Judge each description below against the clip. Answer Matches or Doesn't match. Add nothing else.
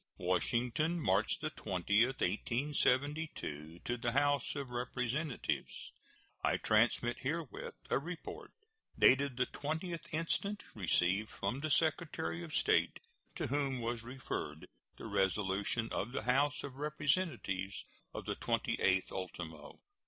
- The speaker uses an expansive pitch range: Matches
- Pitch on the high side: Doesn't match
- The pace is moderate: Doesn't match